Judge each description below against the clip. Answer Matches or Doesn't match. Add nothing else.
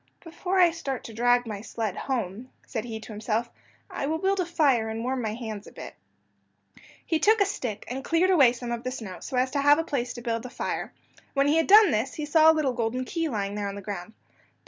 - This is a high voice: Matches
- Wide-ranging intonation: Matches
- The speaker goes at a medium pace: Doesn't match